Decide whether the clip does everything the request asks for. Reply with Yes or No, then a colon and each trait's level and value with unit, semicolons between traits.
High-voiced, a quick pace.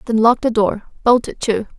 Yes: high, 225 Hz; fast, 235 wpm